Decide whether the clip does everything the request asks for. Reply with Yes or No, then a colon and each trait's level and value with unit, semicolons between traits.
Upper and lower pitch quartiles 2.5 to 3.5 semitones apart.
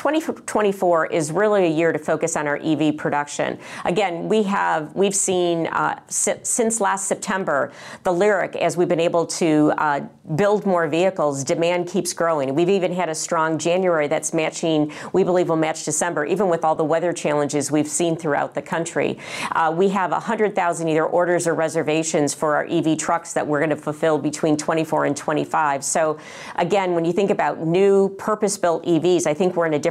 Yes: average, 2.9 semitones